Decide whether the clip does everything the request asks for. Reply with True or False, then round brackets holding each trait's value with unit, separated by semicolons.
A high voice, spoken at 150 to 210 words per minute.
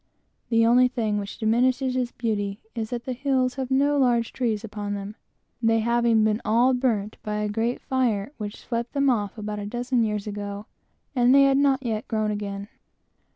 True (230 Hz; 195 wpm)